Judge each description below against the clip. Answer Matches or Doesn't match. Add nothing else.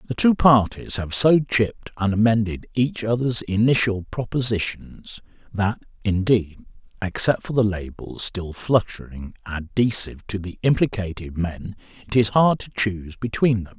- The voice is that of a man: Matches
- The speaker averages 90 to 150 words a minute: Matches